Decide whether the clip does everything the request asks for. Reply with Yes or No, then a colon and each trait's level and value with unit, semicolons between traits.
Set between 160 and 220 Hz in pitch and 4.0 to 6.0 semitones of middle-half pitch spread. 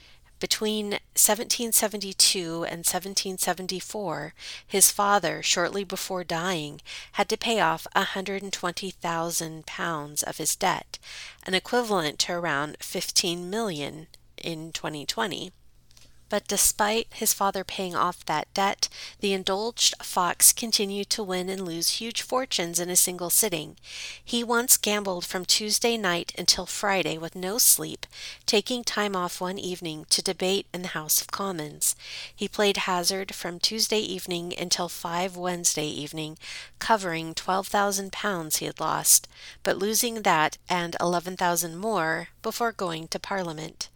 No: medium, 185 Hz; average, 3.2 semitones